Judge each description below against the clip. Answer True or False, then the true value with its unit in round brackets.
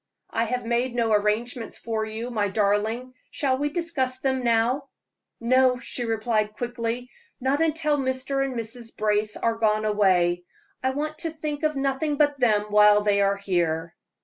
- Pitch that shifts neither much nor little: True (3.9 semitones)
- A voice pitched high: True (235 Hz)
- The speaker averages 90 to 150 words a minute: False (165 wpm)